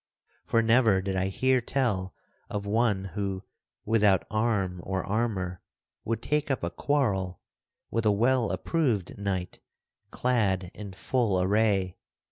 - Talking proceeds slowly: Yes, slow, 130 wpm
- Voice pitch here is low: Yes, low, 105 Hz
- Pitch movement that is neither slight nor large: Yes, average, 3.7 semitones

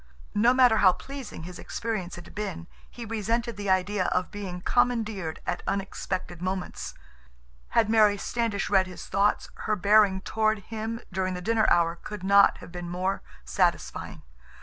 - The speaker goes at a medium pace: Yes, average, 155 wpm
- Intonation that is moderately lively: Yes, average, 3.2 semitones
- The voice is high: Yes, high, 200 Hz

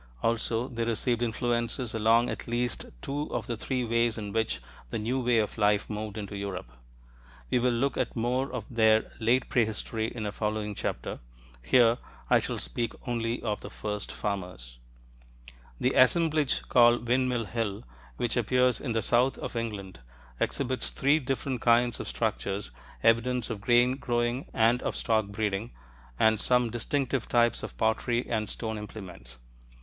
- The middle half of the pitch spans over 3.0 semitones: No, narrow, 2.4 semitones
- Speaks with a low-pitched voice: Yes, low, 115 Hz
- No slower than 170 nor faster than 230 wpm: No, average, 160 wpm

